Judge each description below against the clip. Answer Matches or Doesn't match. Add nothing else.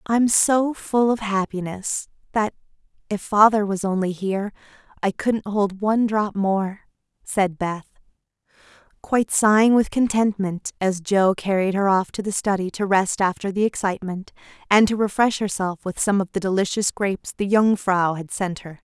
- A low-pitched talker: Doesn't match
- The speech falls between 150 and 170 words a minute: Matches